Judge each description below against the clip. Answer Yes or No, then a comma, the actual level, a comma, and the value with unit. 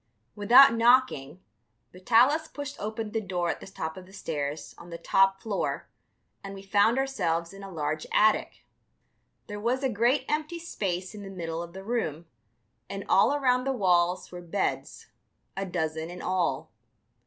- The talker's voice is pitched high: Yes, high, 195 Hz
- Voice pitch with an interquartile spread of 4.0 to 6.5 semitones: Yes, wide, 5.5 semitones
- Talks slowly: No, average, 165 wpm